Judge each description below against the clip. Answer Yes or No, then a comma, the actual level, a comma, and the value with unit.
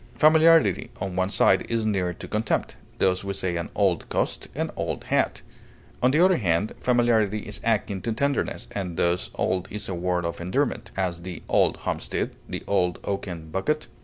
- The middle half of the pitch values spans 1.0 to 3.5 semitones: No, average, 4.2 semitones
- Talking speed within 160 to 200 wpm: Yes, average, 180 wpm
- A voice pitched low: Yes, very low, 95 Hz